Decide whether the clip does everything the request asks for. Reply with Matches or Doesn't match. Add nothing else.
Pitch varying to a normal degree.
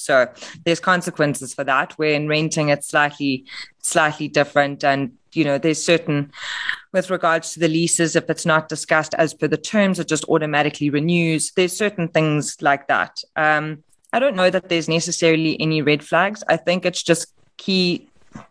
Doesn't match